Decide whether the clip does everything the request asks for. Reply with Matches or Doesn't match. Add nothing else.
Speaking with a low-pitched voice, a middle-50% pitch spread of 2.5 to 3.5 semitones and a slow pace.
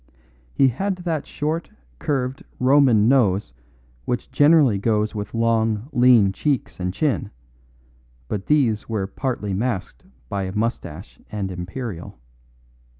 Doesn't match